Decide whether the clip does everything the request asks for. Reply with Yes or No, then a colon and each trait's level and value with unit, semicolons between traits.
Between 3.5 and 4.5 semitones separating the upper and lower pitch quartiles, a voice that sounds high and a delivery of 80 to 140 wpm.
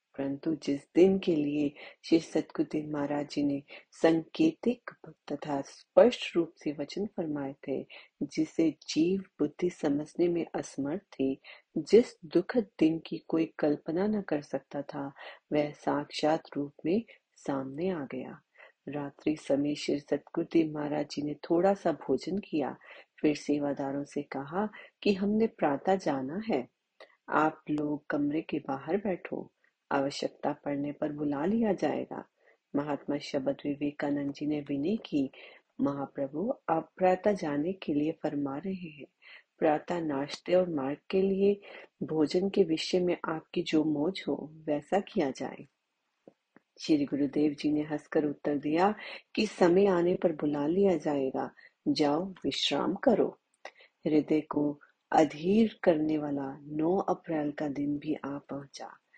No: average, 4.2 semitones; medium, 155 Hz; average, 135 wpm